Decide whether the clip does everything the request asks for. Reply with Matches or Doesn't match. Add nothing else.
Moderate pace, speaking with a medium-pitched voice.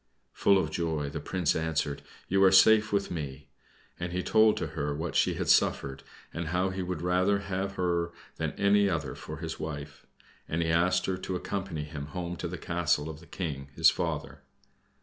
Doesn't match